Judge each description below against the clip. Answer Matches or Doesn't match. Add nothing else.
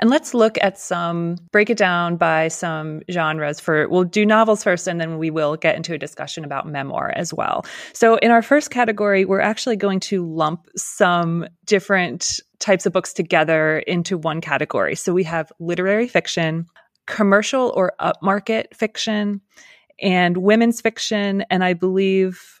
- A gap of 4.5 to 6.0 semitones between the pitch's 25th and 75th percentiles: Doesn't match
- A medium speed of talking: Matches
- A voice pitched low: Doesn't match